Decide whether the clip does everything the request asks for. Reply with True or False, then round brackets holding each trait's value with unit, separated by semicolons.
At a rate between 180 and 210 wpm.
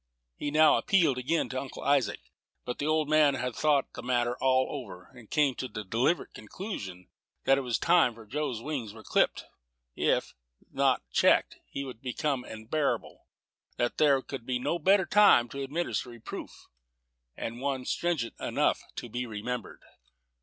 False (165 wpm)